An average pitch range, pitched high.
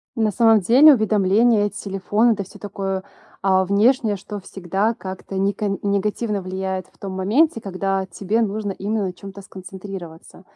No: narrow, 2.1 semitones; high, 200 Hz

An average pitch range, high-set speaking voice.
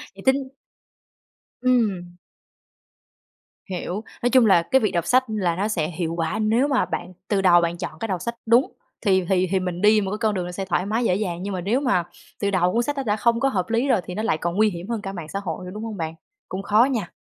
Yes: average, 4.3 semitones; high, 200 Hz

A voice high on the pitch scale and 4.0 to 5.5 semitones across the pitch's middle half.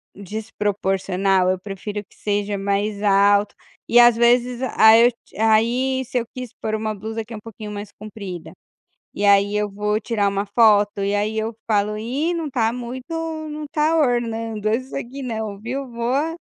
No: high, 220 Hz; average, 2.9 semitones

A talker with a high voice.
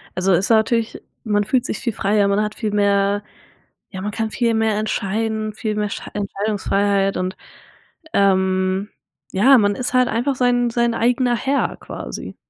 Yes: high, 210 Hz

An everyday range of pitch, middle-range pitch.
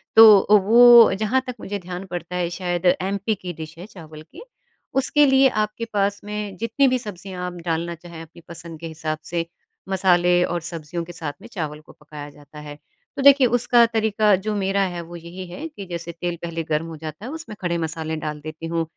Yes: average, 4.3 semitones; medium, 175 Hz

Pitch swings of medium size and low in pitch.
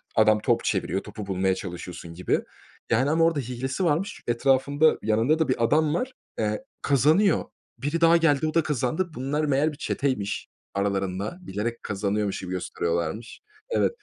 No: wide, 7.2 semitones; low, 130 Hz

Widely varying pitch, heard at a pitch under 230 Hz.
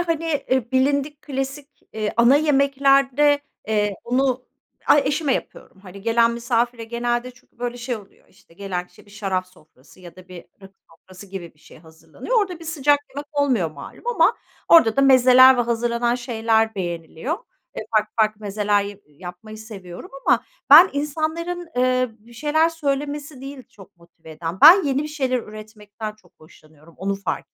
No: wide, 5.9 semitones; high, 235 Hz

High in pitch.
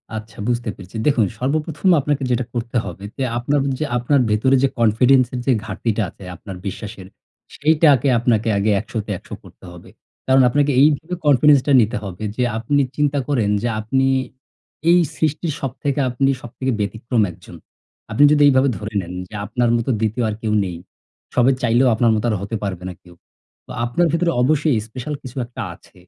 No: low, 120 Hz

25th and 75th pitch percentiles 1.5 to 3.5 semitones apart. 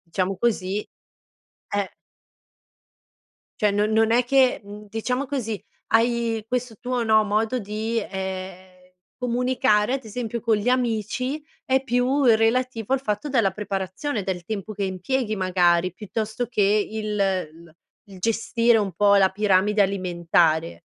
No: average, 3.9 semitones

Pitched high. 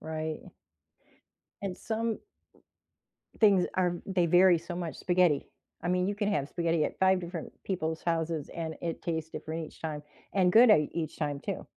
No: medium, 170 Hz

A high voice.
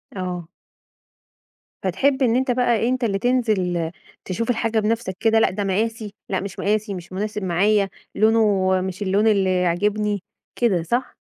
Yes: high, 210 Hz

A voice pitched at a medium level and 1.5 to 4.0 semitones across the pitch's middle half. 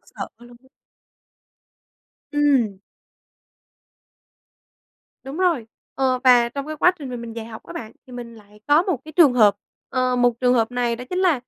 No: very high, 250 Hz; average, 3.6 semitones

